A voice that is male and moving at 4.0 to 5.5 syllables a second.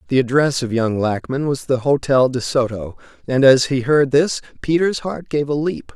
Yes: male; 4.8 syllables/s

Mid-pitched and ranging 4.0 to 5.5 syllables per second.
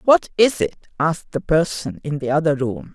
Yes: medium, 160 Hz; 5.2 syllables/s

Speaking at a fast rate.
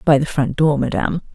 Yes: fast, 225 wpm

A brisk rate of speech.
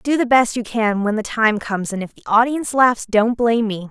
Yes: fast, 260 wpm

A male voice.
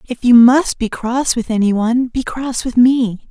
No: female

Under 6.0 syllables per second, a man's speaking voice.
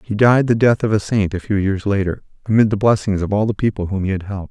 No: 6.4 syllables/s; male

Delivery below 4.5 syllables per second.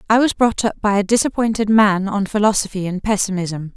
No: 5.6 syllables/s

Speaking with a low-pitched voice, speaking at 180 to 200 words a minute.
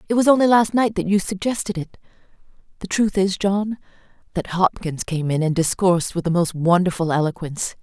No: medium, 185 Hz; average, 185 wpm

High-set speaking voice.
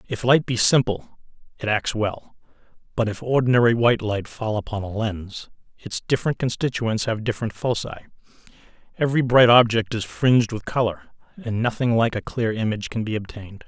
No: low, 115 Hz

